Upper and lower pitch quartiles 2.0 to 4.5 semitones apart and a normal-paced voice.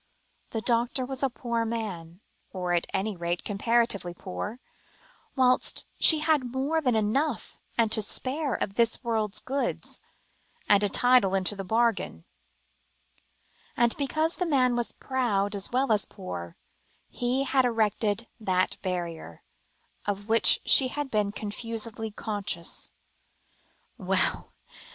No: average, 4.2 semitones; slow, 130 wpm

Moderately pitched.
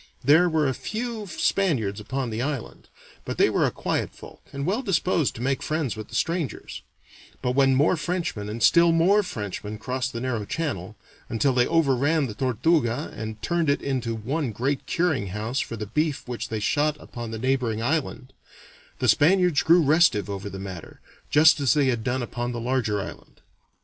No: low, 130 Hz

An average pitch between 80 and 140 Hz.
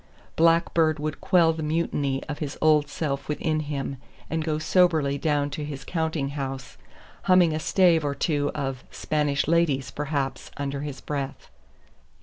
No: medium, 150 Hz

